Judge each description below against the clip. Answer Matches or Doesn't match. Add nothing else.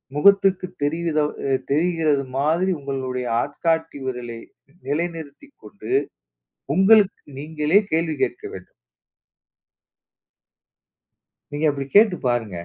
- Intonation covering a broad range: Doesn't match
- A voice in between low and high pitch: Matches